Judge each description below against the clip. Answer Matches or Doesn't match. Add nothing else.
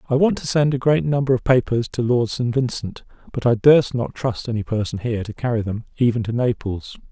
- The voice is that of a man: Matches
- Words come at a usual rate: Doesn't match